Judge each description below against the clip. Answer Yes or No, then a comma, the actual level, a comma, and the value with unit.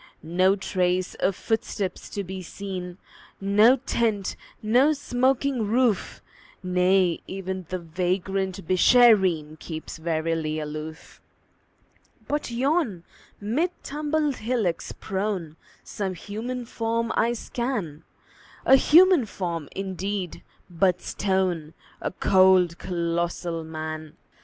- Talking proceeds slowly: Yes, slow, 100 wpm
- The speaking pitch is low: No, high, 190 Hz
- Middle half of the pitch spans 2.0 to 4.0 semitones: No, average, 4.9 semitones